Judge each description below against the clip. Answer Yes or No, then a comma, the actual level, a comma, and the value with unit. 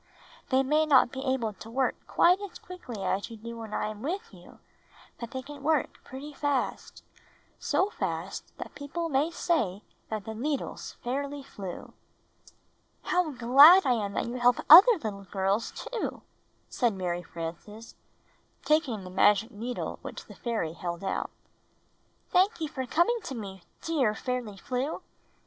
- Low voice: No, very high, 250 Hz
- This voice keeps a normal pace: Yes, average, 160 wpm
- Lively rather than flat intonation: Yes, wide, 6.1 semitones